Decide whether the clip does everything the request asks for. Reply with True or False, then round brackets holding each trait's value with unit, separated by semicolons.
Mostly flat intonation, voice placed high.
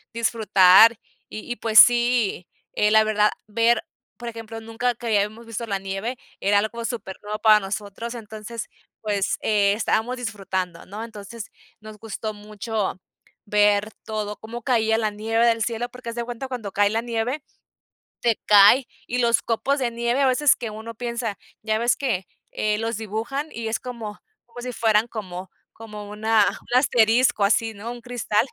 True (2.1 semitones; 225 Hz)